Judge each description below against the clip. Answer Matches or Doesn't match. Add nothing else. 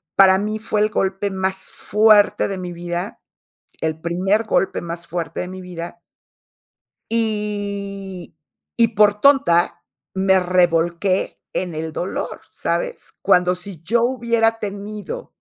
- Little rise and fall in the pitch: Doesn't match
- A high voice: Matches